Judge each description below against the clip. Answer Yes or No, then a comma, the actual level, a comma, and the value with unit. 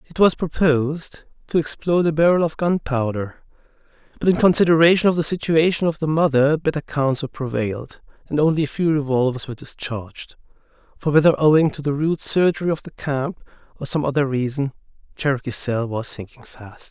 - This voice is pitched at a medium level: Yes, medium, 145 Hz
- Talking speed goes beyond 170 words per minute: No, average, 165 wpm